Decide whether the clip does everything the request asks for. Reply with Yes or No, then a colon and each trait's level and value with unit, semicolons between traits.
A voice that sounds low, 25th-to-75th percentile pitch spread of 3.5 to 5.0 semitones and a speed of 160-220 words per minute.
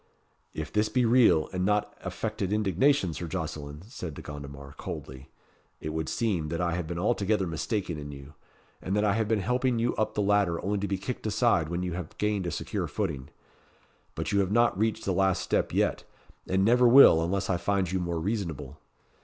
Yes: very low, 95 Hz; average, 4.5 semitones; fast, 205 wpm